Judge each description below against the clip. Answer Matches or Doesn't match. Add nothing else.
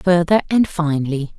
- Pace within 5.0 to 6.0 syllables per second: Doesn't match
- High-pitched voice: Doesn't match